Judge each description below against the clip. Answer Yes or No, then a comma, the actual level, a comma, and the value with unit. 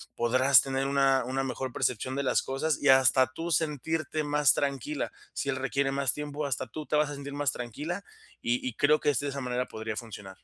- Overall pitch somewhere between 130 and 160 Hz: Yes, low, 135 Hz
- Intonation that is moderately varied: No, narrow, 2.3 semitones